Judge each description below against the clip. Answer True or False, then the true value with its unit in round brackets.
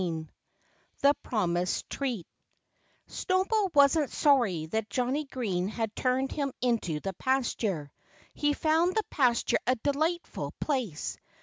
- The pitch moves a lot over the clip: True (6.8 semitones)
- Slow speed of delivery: True (120 wpm)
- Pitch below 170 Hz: False (255 Hz)